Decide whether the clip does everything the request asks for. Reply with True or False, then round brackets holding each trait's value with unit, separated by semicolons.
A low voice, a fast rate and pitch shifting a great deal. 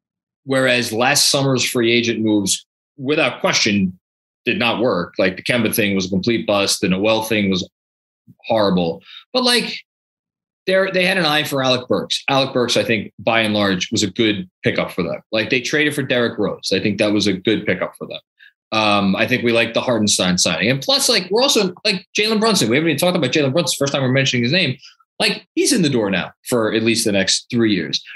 True (120 Hz; 220 wpm; 6.5 semitones)